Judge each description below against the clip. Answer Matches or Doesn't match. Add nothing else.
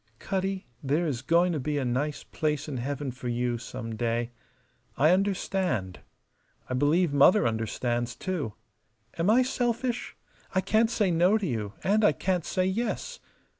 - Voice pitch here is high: Doesn't match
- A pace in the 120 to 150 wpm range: Doesn't match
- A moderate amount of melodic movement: Doesn't match